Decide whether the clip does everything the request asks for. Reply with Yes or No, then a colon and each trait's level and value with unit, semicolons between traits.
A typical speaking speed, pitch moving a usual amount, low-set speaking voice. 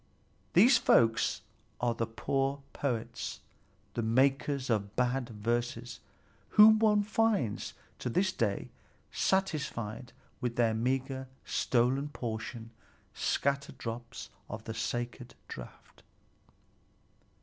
No: slow, 100 wpm; average, 3.4 semitones; low, 125 Hz